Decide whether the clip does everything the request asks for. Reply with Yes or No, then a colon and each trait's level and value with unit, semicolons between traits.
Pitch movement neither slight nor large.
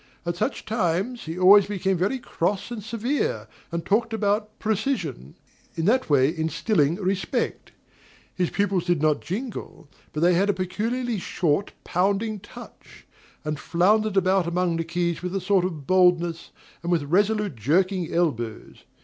Yes: average, 3.7 semitones